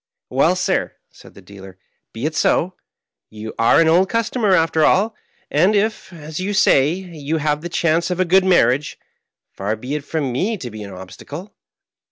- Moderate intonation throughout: No, wide, 6.7 semitones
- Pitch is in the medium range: Yes, medium, 160 Hz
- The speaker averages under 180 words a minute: No, average, 195 wpm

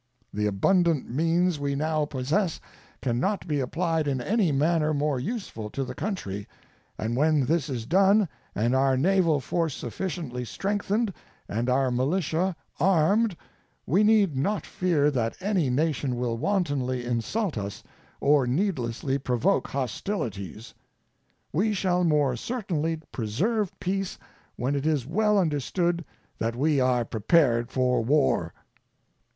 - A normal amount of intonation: No, wide, 6.4 semitones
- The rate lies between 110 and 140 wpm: Yes, slow, 135 wpm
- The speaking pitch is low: No, medium, 150 Hz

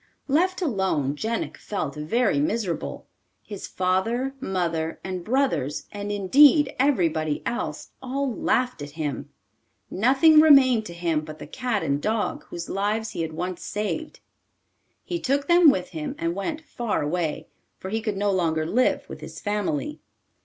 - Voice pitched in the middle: No, high, 205 Hz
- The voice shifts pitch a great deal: Yes, wide, 7.5 semitones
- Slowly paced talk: No, average, 155 wpm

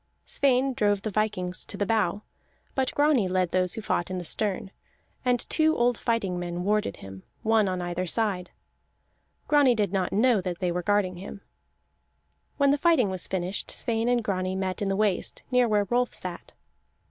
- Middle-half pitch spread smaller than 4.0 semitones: No, average, 4.5 semitones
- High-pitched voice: Yes, high, 205 Hz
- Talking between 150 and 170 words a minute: No, average, 180 wpm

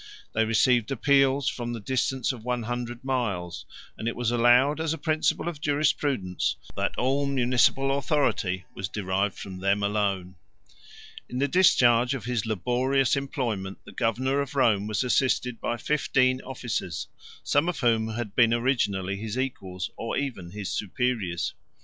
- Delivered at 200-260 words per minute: No, average, 155 wpm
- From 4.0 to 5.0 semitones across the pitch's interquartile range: Yes, average, 4.4 semitones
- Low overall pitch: Yes, low, 120 Hz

